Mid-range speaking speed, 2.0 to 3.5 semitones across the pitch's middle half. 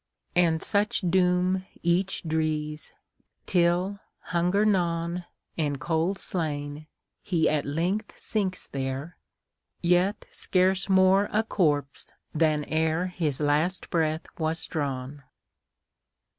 No: slow, 90 wpm; average, 3.2 semitones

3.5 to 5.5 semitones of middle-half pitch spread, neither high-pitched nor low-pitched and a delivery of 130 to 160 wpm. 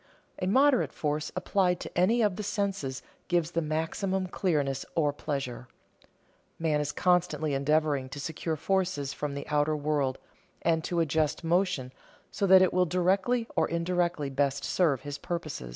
Yes: average, 4.1 semitones; medium, 160 Hz; average, 155 wpm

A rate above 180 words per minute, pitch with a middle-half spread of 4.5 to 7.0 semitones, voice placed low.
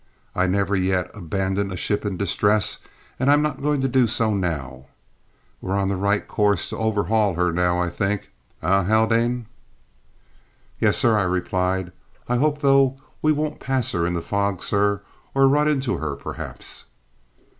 No: average, 165 wpm; average, 4.9 semitones; low, 100 Hz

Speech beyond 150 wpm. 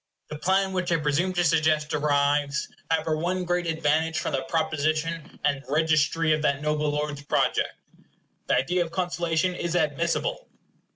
Yes: average, 160 wpm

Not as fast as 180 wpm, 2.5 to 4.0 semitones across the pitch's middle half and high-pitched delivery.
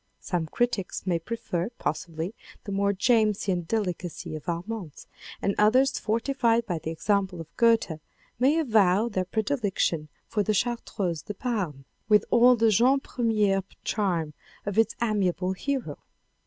No: average, 140 wpm; average, 4.5 semitones; high, 205 Hz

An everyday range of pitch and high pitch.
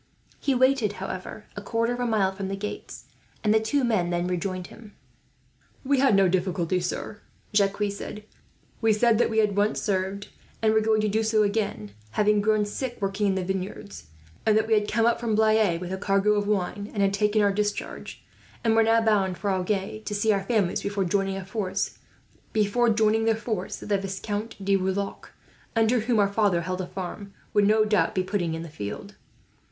No: narrow, 2.2 semitones; high, 205 Hz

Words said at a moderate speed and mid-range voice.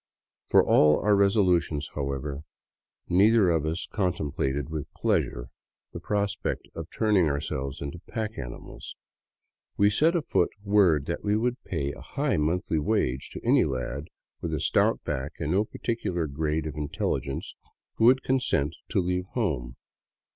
No: average, 145 wpm; very low, 85 Hz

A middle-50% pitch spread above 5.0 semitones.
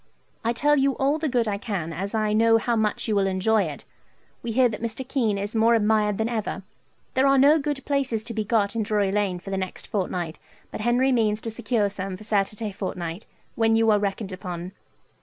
No: average, 3.0 semitones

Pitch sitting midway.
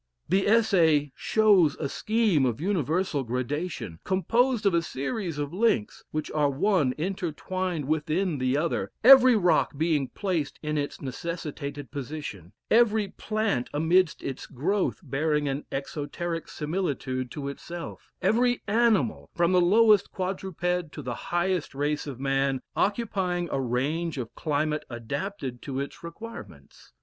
Yes: medium, 160 Hz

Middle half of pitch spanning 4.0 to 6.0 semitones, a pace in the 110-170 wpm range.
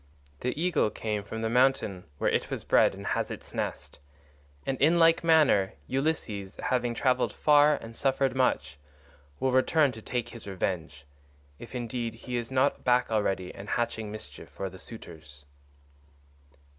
Yes: average, 5.2 semitones; average, 155 wpm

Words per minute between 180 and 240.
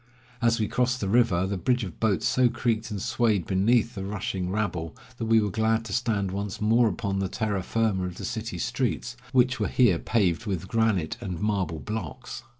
Yes: average, 200 wpm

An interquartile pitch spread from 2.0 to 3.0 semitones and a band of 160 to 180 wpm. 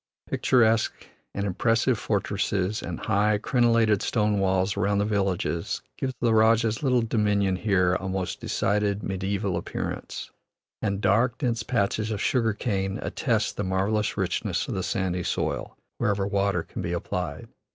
No: narrow, 2.4 semitones; average, 145 wpm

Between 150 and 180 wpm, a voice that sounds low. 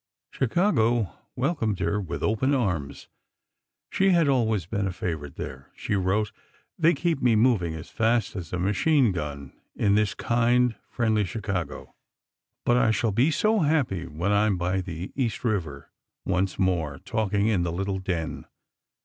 Yes: average, 160 wpm; low, 105 Hz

